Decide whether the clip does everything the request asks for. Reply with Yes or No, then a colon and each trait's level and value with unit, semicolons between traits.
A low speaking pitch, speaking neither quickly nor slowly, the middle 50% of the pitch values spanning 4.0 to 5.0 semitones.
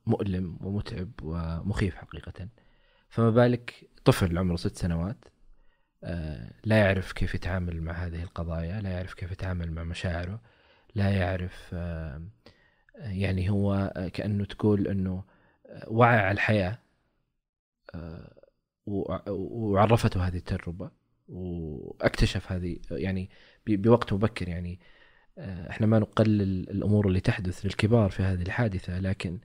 No: very low, 95 Hz; average, 110 wpm; average, 2.8 semitones